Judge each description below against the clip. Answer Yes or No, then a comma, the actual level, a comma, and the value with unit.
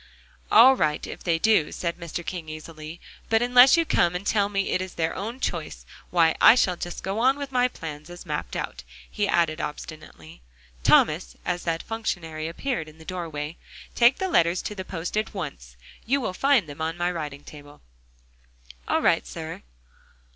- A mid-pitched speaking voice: Yes, medium, 175 Hz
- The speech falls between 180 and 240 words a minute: Yes, average, 185 wpm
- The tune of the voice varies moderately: No, wide, 5.7 semitones